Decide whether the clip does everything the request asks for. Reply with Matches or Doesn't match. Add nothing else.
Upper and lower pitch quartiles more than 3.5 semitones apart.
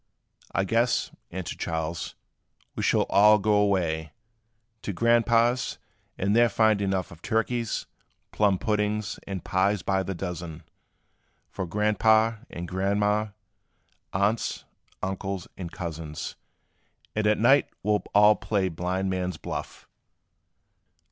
Doesn't match